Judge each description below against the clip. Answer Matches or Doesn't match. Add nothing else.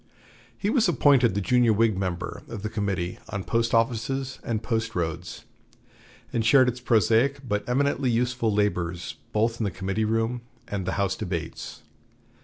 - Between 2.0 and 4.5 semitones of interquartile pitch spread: Matches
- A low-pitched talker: Matches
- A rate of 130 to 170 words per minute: Matches